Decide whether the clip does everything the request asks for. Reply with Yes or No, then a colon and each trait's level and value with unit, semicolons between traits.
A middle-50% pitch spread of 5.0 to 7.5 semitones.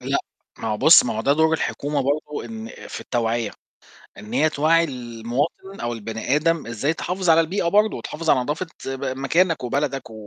Yes: wide, 5.4 semitones